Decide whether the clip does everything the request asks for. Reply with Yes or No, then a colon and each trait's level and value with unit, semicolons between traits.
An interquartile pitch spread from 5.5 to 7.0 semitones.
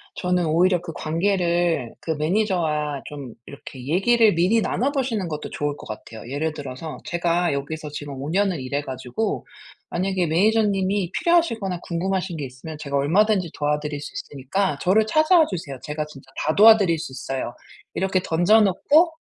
No: average, 5.1 semitones